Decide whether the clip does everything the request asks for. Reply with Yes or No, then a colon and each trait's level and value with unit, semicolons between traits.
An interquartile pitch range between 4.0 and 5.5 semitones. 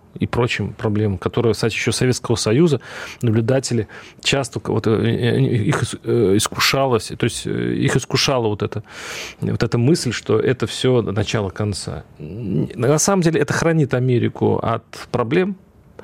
No: average, 3.3 semitones